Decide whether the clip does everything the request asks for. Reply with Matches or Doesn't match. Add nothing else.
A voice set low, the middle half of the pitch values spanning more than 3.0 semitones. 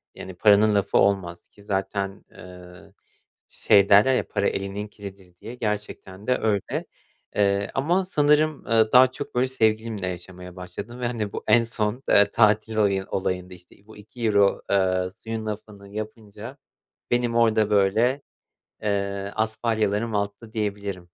Doesn't match